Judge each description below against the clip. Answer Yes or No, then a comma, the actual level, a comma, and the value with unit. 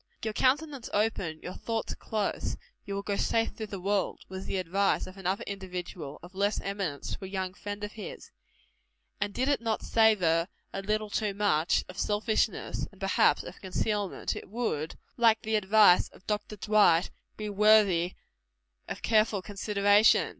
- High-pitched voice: Yes, high, 205 Hz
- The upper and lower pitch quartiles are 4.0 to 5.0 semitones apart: No, narrow, 2.4 semitones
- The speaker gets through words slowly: No, average, 165 wpm